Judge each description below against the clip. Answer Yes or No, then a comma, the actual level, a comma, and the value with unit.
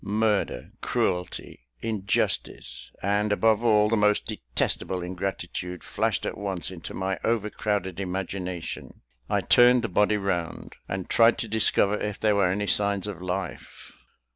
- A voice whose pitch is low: Yes, low, 100 Hz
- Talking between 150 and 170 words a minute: No, average, 140 wpm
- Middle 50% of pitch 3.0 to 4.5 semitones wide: No, narrow, 2.4 semitones